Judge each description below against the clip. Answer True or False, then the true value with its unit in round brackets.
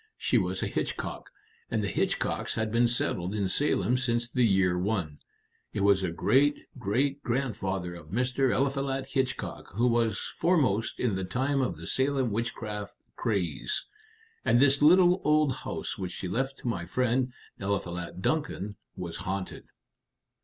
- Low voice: True (115 Hz)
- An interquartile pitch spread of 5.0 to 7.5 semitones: True (5.6 semitones)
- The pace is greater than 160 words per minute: False (155 wpm)